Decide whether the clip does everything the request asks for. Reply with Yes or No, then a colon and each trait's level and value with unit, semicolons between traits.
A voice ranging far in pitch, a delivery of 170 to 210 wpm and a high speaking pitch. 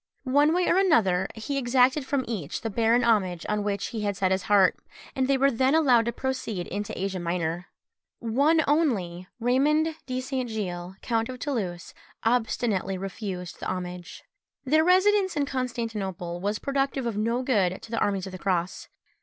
Yes: wide, 5.9 semitones; average, 180 wpm; high, 230 Hz